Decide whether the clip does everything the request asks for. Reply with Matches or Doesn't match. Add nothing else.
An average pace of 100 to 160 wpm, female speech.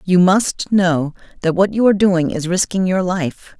Doesn't match